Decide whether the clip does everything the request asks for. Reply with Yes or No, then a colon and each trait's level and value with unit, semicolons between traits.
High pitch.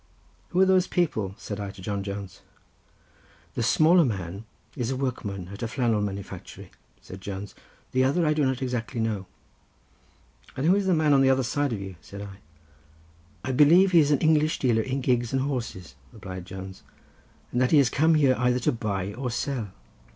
No: low, 125 Hz